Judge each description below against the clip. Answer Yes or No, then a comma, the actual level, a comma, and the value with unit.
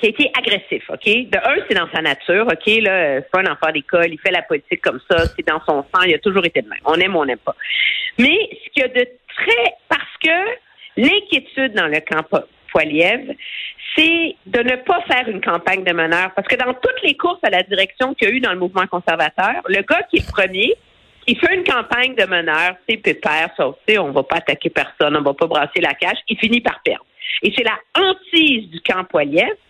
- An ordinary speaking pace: No, fast, 245 wpm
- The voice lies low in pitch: No, high, 225 Hz